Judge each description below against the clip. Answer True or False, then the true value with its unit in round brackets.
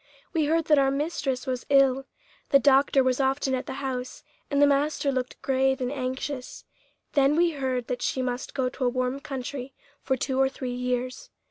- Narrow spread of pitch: True (1.6 semitones)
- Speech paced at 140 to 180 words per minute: False (195 wpm)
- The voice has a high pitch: True (265 Hz)